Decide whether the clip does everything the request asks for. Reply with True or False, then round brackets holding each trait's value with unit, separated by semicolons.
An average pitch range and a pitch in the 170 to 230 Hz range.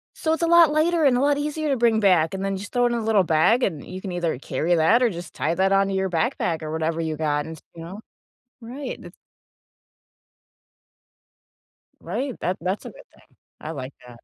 False (7.3 semitones; 190 Hz)